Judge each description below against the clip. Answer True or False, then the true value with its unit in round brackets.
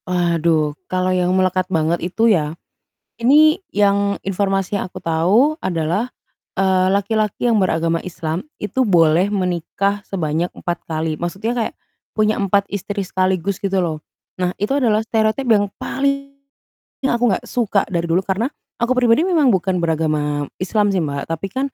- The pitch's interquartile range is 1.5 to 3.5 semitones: False (4.1 semitones)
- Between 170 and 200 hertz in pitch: True (190 Hz)